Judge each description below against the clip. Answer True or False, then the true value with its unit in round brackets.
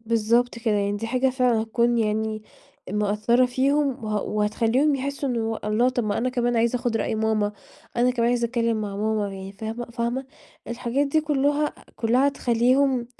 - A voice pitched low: False (235 Hz)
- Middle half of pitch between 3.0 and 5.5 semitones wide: False (2.6 semitones)